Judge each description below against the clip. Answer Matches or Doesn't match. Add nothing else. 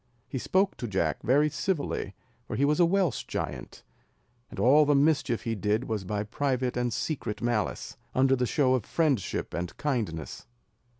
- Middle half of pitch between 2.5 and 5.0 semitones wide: Doesn't match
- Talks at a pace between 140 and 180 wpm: Matches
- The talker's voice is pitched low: Matches